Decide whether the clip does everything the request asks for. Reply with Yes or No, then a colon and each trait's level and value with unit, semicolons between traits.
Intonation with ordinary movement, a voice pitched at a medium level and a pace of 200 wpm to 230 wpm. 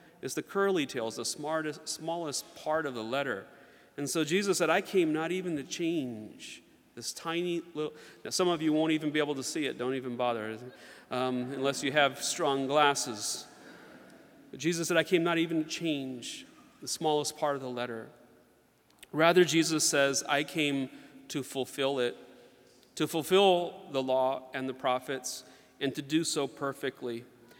No: average, 3.9 semitones; medium, 145 Hz; average, 170 wpm